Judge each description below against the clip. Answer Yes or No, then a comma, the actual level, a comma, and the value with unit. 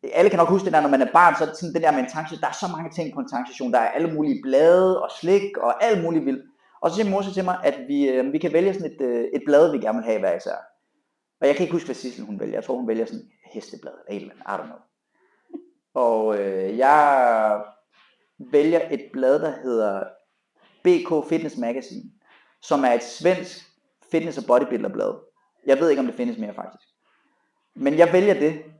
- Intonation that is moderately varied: No, wide, 7.8 semitones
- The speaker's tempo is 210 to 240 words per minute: Yes, average, 220 wpm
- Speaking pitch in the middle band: Yes, medium, 170 Hz